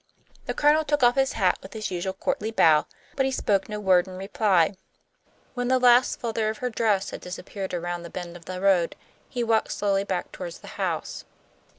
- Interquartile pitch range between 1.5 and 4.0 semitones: No, average, 4.6 semitones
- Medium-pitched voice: No, high, 200 Hz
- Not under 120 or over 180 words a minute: No, fast, 205 wpm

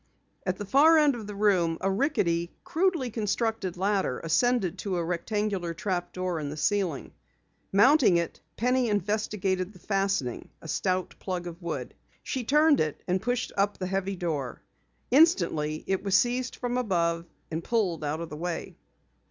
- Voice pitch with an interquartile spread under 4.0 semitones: No, average, 4.9 semitones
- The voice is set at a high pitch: Yes, high, 195 Hz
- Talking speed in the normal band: Yes, average, 165 wpm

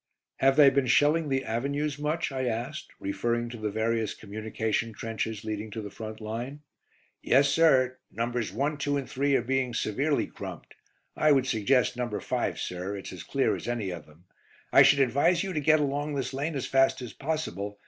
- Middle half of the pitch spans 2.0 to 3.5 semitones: No, average, 4.3 semitones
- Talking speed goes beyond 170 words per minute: Yes, average, 190 wpm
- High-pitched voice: No, low, 130 Hz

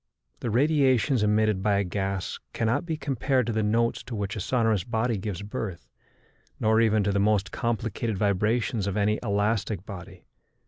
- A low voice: Yes, low, 110 Hz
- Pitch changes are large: No, narrow, 2.6 semitones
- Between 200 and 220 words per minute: No, average, 170 wpm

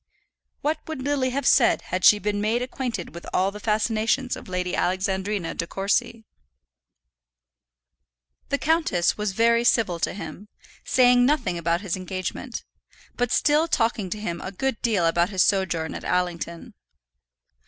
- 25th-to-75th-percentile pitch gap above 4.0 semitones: Yes, average, 5.2 semitones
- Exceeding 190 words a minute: No, average, 150 wpm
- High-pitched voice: Yes, high, 210 Hz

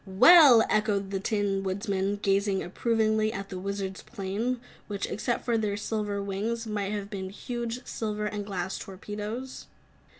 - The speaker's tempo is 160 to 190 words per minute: No, average, 145 wpm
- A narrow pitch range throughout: Yes, narrow, 2.2 semitones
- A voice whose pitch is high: Yes, high, 205 Hz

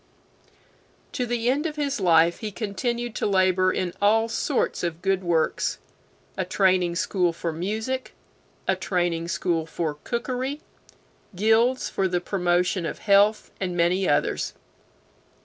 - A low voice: No, high, 190 Hz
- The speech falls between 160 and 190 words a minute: No, average, 140 wpm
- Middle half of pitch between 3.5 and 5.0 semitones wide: Yes, average, 4.6 semitones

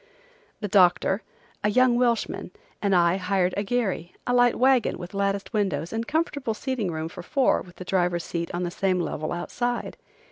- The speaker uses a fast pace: No, average, 180 wpm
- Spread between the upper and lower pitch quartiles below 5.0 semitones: No, wide, 5.4 semitones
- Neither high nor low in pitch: No, high, 195 Hz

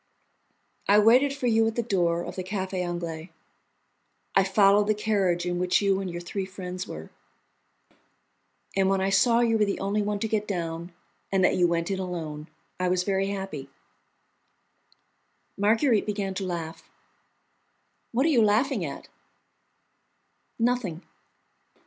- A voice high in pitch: Yes, high, 195 Hz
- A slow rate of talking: No, average, 150 wpm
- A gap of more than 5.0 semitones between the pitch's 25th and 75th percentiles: No, average, 3.1 semitones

